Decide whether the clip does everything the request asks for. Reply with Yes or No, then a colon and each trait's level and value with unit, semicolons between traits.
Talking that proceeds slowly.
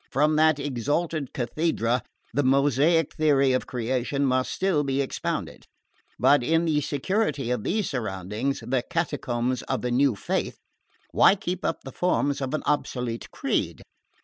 No: average, 150 wpm